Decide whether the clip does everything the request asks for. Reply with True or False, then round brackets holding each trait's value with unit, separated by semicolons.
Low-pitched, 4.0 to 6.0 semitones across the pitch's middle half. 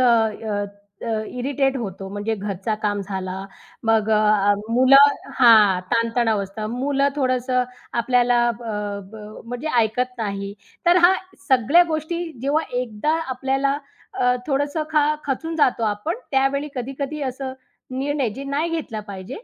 False (250 Hz; 4.4 semitones)